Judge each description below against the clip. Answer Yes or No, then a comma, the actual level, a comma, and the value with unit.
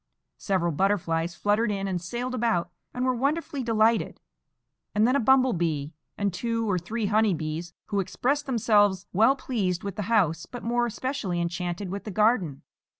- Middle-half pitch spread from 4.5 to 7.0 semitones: Yes, average, 5.1 semitones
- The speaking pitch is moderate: No, high, 205 Hz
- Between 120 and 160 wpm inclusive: No, average, 170 wpm